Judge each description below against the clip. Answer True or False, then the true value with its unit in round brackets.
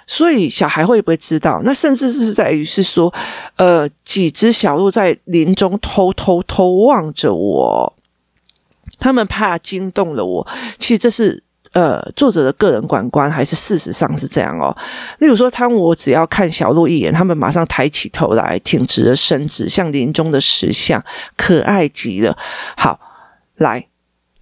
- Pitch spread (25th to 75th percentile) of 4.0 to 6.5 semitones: True (5.6 semitones)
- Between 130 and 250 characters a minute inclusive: True (235 characters per minute)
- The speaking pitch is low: False (185 Hz)